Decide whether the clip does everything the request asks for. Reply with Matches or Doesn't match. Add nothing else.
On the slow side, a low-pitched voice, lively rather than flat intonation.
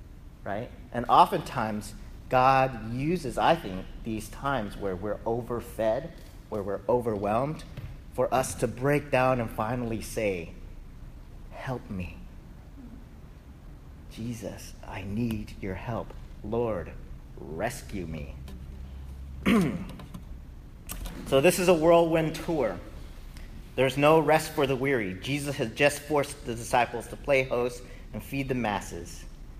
Matches